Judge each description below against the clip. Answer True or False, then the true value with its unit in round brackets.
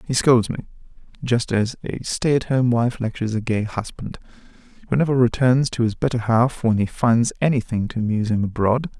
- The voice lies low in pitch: True (120 Hz)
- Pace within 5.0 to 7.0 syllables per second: True (5.5 syllables/s)